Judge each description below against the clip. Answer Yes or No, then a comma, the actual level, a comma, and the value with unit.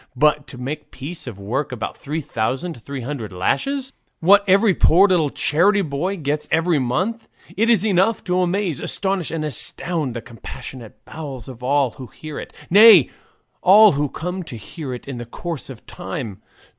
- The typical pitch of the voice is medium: Yes, medium, 150 Hz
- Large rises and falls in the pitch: Yes, wide, 6.1 semitones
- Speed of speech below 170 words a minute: No, average, 175 wpm